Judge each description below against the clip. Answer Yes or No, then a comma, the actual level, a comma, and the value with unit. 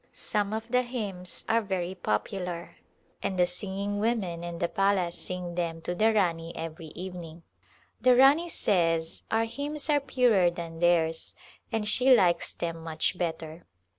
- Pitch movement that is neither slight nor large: Yes, average, 4.7 semitones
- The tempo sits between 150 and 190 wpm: Yes, average, 155 wpm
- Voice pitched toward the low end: No, medium, 180 Hz